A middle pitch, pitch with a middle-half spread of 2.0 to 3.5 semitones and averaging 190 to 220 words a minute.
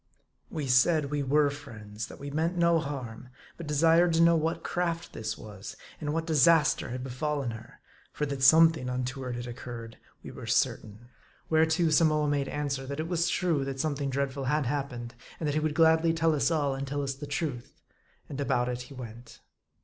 No: medium, 145 Hz; average, 4.0 semitones; average, 195 wpm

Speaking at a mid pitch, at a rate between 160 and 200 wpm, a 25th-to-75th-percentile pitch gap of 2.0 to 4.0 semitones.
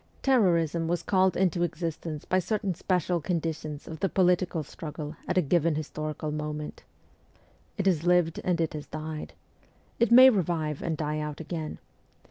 No: medium, 165 Hz; average, 150 wpm; average, 2.9 semitones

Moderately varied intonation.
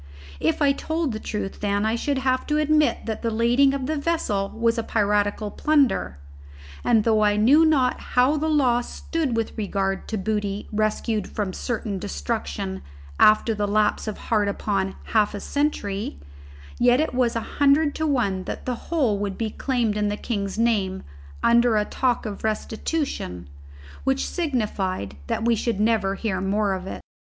Yes: average, 4.2 semitones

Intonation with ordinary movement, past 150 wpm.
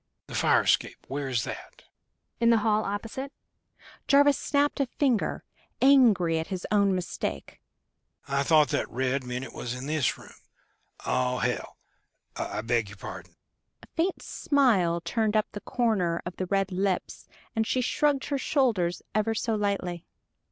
No: wide, 7.2 semitones; average, 160 wpm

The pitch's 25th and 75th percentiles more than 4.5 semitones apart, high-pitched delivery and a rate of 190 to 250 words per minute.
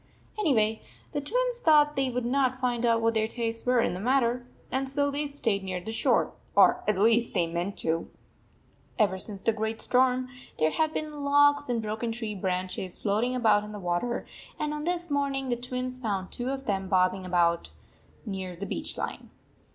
Yes: average, 5.2 semitones; high, 235 Hz; fast, 205 wpm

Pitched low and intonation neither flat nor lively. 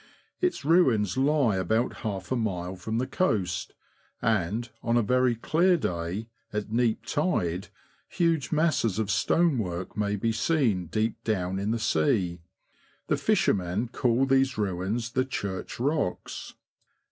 No: low, 110 Hz; wide, 5.7 semitones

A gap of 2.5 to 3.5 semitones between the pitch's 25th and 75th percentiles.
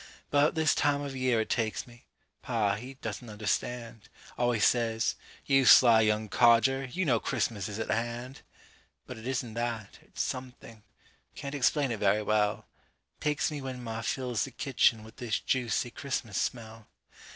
Yes: average, 2.9 semitones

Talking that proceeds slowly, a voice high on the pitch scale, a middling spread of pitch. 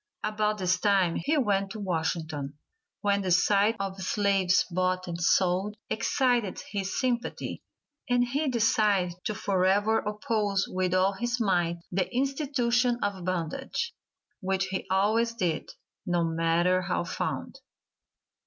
Yes: slow, 130 wpm; high, 195 Hz; average, 3.4 semitones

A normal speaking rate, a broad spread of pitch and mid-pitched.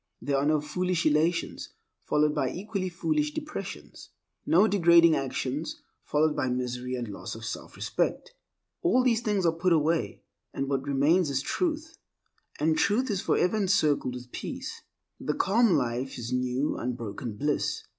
Yes: average, 150 wpm; wide, 6.5 semitones; medium, 155 Hz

